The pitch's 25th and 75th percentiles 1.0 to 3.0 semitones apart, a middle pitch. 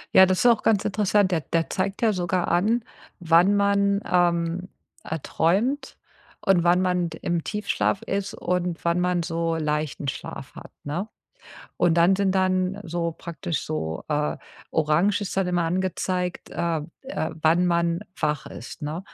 Yes: narrow, 2.6 semitones; medium, 175 Hz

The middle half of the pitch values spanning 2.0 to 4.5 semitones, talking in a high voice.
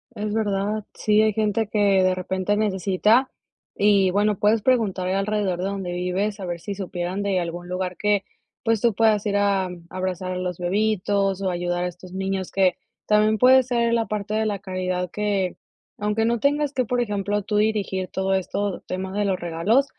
Yes: narrow, 2.4 semitones; high, 200 Hz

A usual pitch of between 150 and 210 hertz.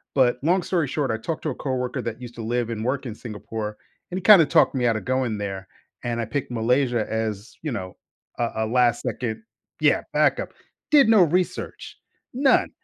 No: low, 125 Hz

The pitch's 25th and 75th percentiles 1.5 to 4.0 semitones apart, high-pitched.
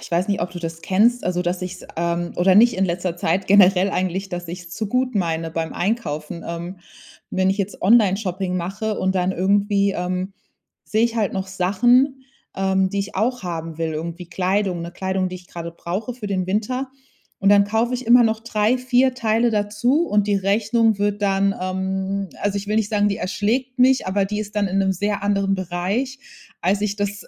Yes: average, 2.8 semitones; high, 195 Hz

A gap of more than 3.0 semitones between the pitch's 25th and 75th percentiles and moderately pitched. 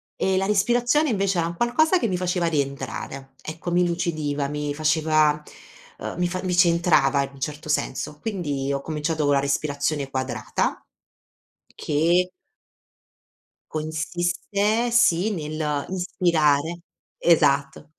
Yes: average, 3.9 semitones; medium, 160 Hz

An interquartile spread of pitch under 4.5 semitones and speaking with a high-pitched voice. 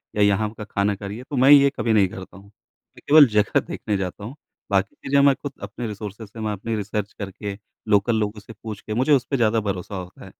No: narrow, 2.5 semitones; low, 105 Hz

